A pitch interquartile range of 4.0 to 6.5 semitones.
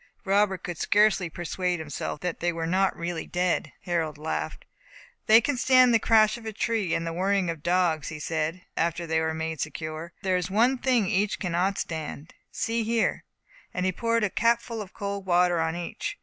Yes: average, 4.3 semitones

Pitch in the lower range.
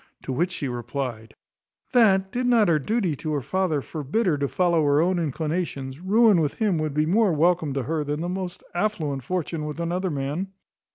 No: medium, 165 Hz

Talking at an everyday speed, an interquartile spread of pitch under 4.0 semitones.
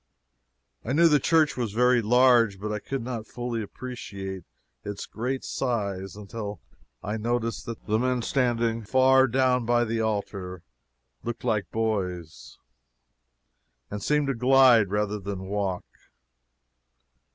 No: slow, 130 wpm; average, 3.5 semitones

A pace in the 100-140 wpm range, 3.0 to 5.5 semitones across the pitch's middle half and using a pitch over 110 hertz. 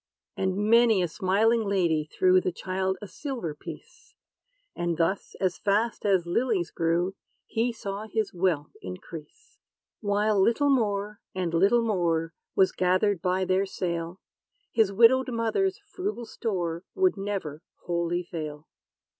Yes: slow, 135 wpm; average, 4.2 semitones; high, 190 Hz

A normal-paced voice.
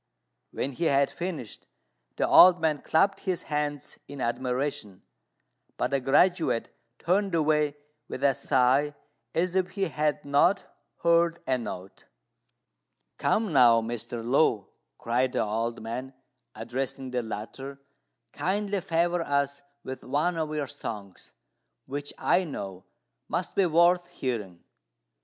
No: slow, 130 wpm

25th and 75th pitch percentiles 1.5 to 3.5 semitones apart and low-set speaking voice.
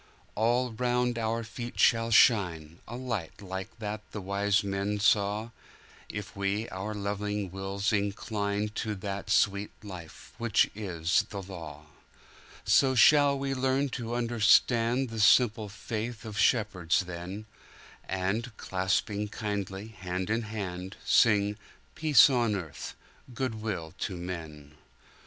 Yes: average, 3.1 semitones; low, 105 Hz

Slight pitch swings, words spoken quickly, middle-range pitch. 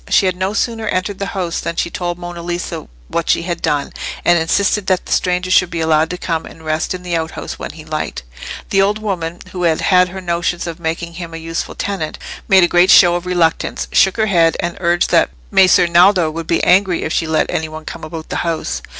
Yes: narrow, 1.9 semitones; fast, 235 wpm; medium, 175 Hz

